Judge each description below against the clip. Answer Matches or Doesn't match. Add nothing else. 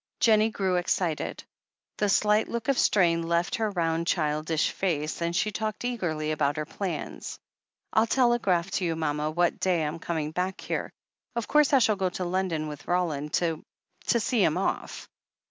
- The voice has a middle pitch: Matches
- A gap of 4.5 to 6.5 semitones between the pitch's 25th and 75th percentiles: Matches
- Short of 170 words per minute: Doesn't match